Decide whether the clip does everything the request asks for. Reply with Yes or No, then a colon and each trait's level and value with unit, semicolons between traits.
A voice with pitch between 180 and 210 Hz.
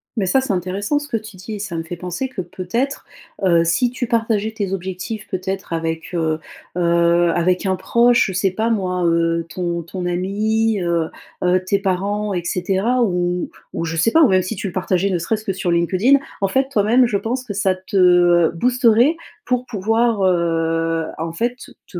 Yes: high, 190 Hz